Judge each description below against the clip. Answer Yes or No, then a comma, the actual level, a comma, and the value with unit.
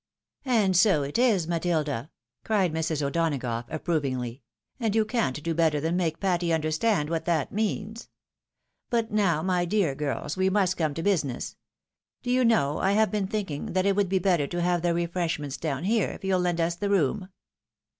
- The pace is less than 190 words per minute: No, average, 195 wpm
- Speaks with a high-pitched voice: No, medium, 175 Hz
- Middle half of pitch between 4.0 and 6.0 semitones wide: Yes, average, 4.5 semitones